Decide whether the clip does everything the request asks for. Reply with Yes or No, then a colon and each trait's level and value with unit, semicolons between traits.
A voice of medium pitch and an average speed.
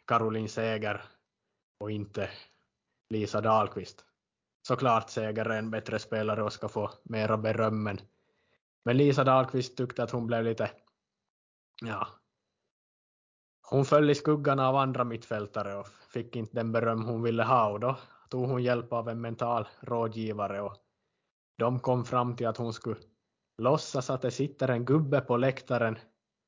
No: low, 115 Hz; average, 150 wpm